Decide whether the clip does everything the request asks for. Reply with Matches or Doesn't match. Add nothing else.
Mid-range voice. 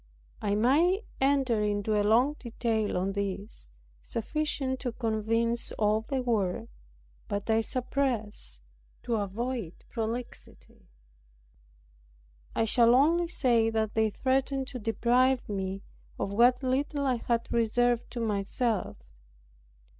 Doesn't match